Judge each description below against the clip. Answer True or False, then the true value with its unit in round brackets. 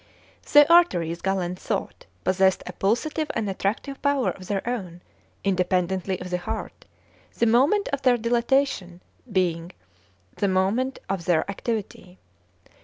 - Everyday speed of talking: False (130 wpm)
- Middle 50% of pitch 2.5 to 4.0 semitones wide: False (5.2 semitones)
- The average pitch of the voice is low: False (195 Hz)